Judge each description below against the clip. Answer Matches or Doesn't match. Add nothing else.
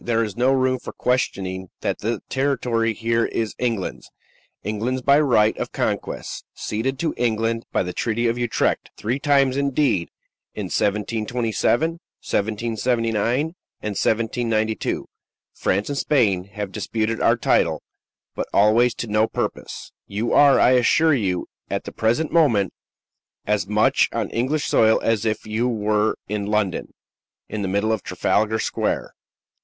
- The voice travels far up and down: Doesn't match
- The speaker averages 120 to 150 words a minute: Matches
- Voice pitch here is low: Matches